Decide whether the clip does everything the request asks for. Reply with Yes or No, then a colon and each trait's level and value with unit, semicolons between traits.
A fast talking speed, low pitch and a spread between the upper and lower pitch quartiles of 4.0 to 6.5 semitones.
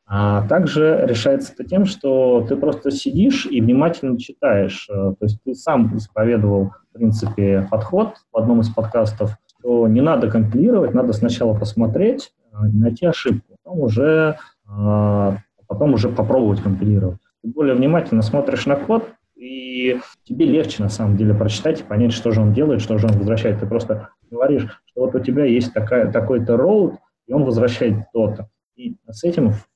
Yes: fast, 165 wpm; low, 115 Hz; average, 4.6 semitones